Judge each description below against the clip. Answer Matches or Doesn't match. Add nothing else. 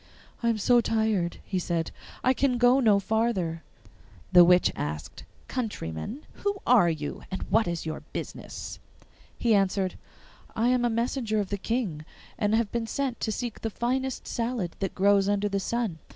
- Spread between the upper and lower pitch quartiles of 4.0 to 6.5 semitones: Matches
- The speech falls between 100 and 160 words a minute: Doesn't match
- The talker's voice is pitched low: Doesn't match